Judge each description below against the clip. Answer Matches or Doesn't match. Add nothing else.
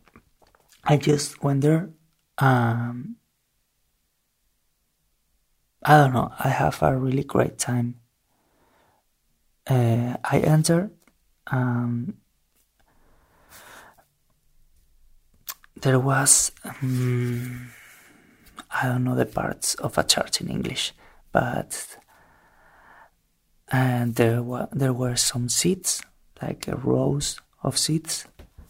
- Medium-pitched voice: Doesn't match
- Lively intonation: Doesn't match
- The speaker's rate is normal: Doesn't match